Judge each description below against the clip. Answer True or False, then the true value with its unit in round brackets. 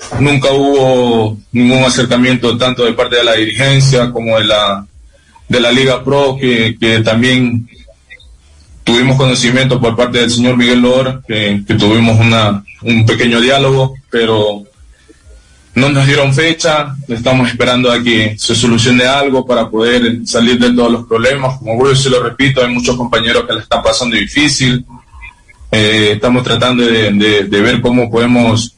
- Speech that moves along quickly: False (160 wpm)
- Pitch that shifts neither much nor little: False (2.2 semitones)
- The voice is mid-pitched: False (120 Hz)